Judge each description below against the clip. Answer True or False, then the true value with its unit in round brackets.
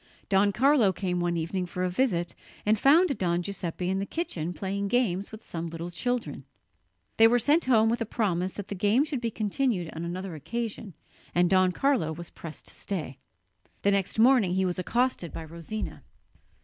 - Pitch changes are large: False (4.8 semitones)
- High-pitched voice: True (195 Hz)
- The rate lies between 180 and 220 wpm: True (190 wpm)